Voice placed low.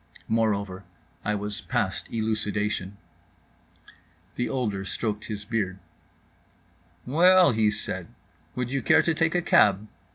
Yes: low, 110 Hz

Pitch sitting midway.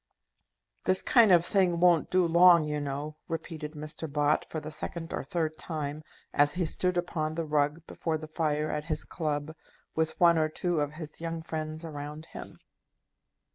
Yes: medium, 155 Hz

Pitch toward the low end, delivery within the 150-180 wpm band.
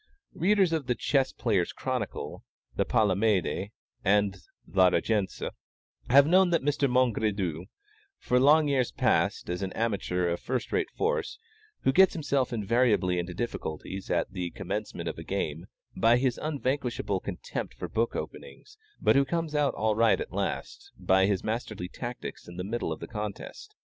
Yes: low, 115 Hz; average, 160 wpm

